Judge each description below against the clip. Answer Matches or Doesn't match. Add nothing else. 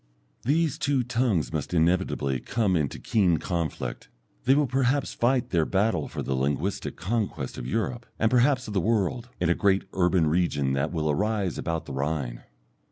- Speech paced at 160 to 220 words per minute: Matches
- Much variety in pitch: Matches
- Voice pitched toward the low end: Matches